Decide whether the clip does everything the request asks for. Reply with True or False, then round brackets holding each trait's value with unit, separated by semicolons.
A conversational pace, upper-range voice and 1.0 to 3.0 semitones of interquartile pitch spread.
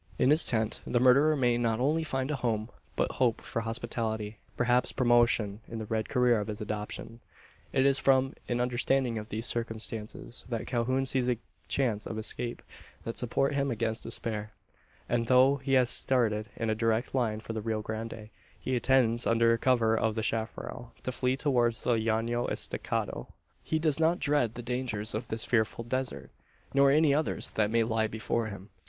False (185 wpm; 120 Hz; 2.7 semitones)